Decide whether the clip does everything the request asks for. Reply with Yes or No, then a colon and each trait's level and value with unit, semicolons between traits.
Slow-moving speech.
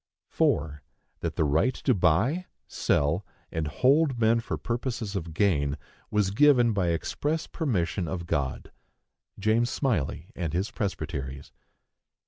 Yes: slow, 125 wpm